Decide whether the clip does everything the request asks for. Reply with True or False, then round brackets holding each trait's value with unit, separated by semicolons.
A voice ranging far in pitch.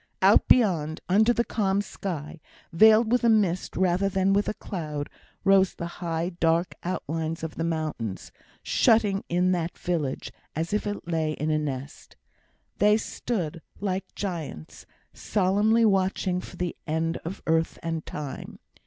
False (3.7 semitones)